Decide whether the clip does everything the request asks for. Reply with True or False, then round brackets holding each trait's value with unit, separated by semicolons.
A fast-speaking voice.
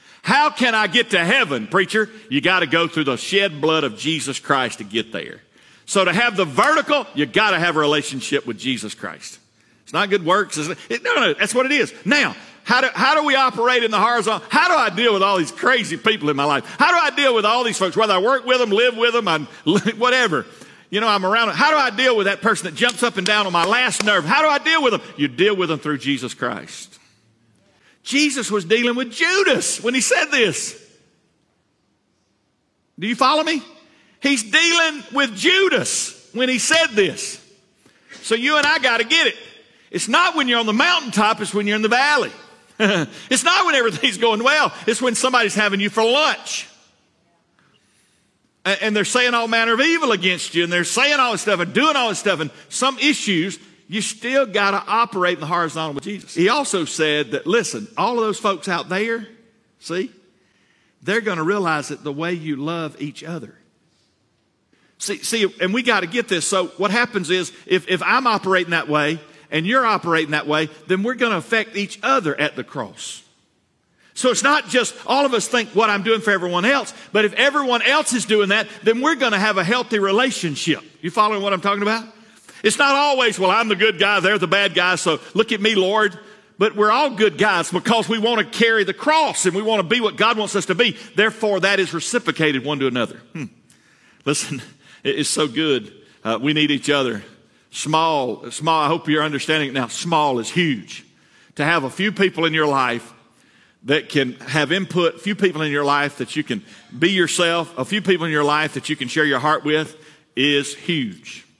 True (215 wpm)